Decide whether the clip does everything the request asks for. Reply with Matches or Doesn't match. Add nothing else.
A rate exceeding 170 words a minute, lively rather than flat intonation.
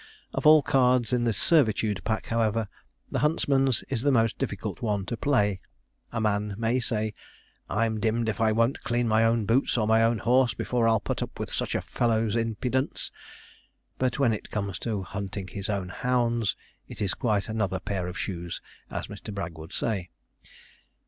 Doesn't match